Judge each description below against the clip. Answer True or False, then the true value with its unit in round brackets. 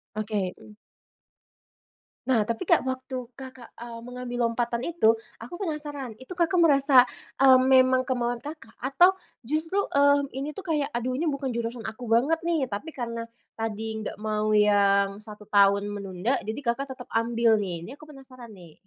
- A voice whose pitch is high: True (245 Hz)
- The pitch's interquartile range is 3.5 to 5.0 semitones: True (4.1 semitones)